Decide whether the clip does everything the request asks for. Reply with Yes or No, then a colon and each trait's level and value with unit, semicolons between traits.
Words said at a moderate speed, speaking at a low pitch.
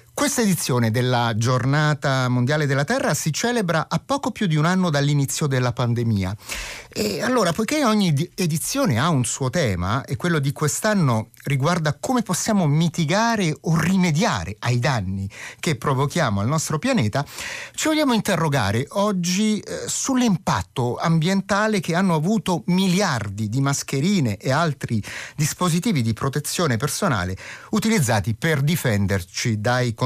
No: average, 135 wpm; medium, 150 Hz